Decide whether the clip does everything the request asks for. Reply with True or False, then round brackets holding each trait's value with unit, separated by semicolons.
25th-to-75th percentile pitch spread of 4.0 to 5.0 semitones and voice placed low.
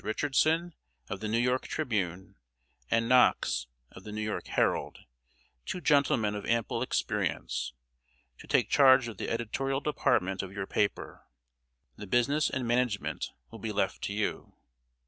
True (4.3 semitones; 115 Hz)